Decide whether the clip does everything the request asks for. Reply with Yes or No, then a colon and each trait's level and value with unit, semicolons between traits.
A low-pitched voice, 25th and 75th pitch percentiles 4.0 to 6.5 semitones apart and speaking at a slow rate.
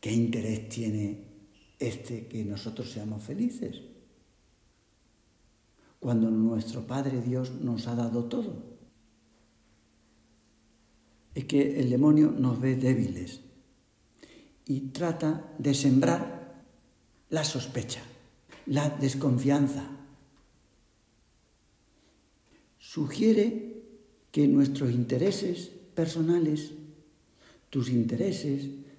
Yes: low, 130 Hz; average, 4.4 semitones; slow, 80 wpm